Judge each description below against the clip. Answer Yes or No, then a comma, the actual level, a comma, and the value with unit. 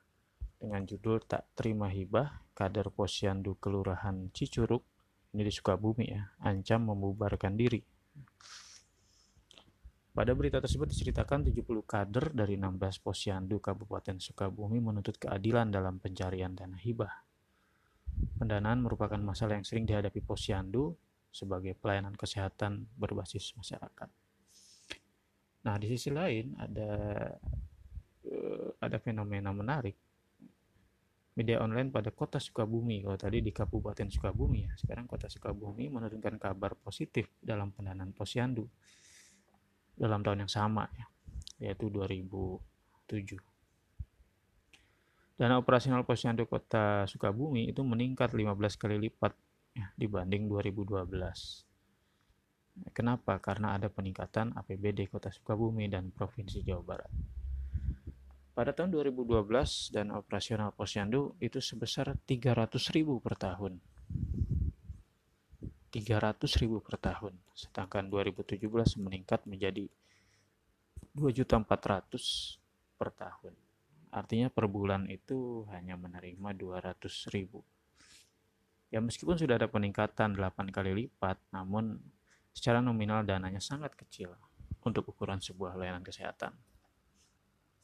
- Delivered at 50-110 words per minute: Yes, average, 105 wpm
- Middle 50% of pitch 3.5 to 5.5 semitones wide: No, average, 2.9 semitones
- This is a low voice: Yes, low, 105 Hz